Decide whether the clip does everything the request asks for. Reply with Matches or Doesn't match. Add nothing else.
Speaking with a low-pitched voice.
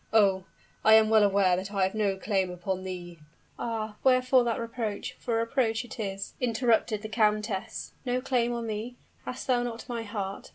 Doesn't match